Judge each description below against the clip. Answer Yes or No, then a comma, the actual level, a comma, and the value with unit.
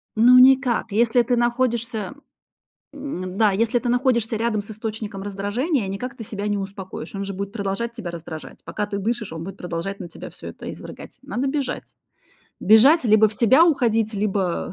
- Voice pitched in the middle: No, high, 220 Hz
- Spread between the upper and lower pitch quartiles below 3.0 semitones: No, average, 3.4 semitones